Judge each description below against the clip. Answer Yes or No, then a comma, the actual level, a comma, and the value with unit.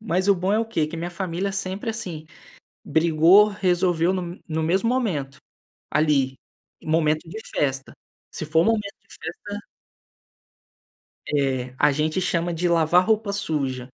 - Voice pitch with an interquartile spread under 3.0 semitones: No, average, 3.8 semitones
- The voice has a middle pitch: Yes, medium, 170 Hz